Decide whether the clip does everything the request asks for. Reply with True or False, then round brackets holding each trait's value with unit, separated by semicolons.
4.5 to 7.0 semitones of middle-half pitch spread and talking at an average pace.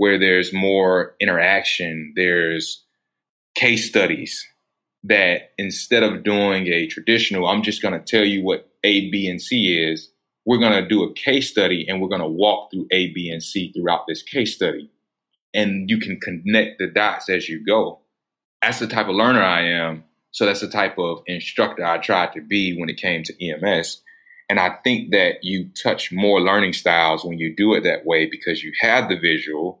False (3.2 semitones; 190 wpm)